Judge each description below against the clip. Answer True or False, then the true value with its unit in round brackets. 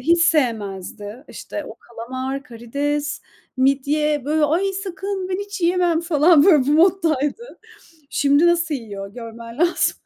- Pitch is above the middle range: True (295 Hz)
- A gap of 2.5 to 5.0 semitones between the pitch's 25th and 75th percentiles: False (5.4 semitones)